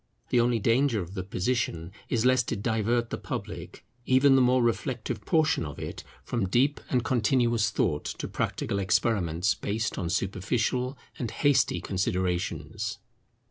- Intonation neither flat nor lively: Yes, average, 4.5 semitones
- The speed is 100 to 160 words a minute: Yes, average, 145 wpm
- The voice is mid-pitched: No, low, 115 Hz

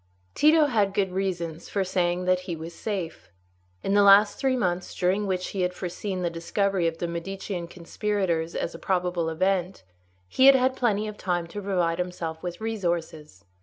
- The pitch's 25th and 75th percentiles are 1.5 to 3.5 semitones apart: Yes, average, 2.8 semitones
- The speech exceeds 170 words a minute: Yes, average, 180 wpm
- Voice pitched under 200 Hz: Yes, medium, 185 Hz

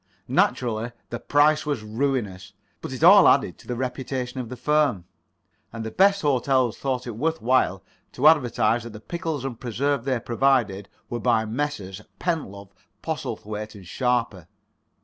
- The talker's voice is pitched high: No, low, 125 Hz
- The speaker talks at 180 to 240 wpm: No, average, 155 wpm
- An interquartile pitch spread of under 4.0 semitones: No, average, 4.3 semitones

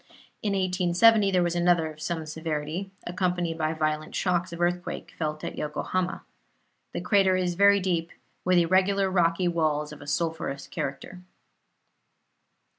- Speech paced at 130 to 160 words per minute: Yes, average, 140 wpm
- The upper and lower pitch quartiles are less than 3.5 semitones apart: Yes, average, 2.8 semitones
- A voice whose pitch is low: No, medium, 175 Hz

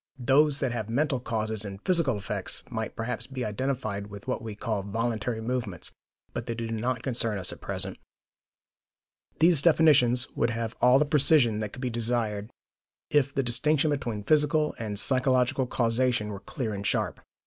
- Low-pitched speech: Yes, low, 120 Hz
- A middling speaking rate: Yes, average, 170 wpm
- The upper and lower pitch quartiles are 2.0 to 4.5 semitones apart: Yes, average, 3.6 semitones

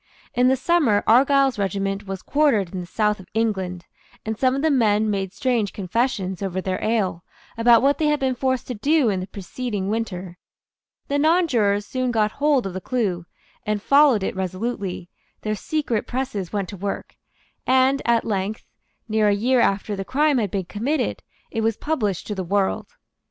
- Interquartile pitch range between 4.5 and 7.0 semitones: Yes, average, 4.9 semitones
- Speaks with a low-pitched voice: No, high, 215 Hz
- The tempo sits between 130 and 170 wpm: No, average, 185 wpm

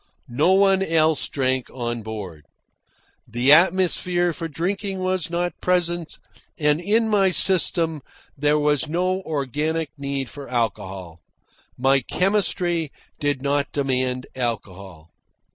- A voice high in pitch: No, medium, 150 Hz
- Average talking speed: No, slow, 115 wpm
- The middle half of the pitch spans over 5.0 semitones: Yes, wide, 5.6 semitones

